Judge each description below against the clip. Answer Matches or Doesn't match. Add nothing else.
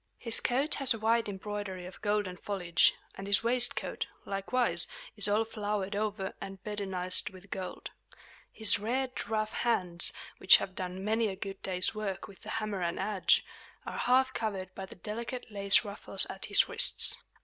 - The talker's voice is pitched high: Matches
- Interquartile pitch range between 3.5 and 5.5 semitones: Doesn't match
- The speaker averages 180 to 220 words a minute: Doesn't match